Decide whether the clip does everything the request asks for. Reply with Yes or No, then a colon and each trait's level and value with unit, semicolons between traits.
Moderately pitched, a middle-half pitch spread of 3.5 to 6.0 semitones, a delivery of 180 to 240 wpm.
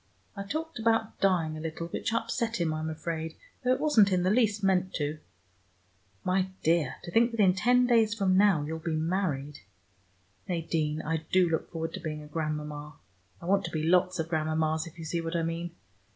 Yes: medium, 170 Hz; average, 3.9 semitones; average, 200 wpm